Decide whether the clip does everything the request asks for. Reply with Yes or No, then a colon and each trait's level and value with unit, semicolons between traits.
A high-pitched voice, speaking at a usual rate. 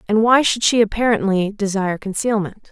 Yes: high, 210 Hz; average, 155 wpm